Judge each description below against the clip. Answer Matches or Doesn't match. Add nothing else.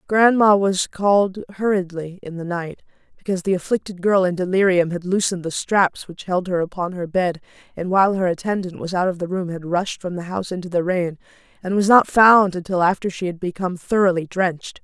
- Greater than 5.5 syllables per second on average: Matches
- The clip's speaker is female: Matches